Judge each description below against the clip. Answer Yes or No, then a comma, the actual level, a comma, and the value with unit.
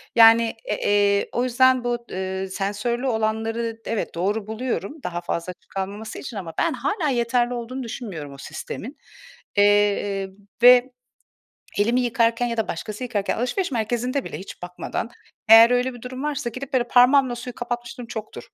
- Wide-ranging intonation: No, average, 3.4 semitones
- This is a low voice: No, high, 230 Hz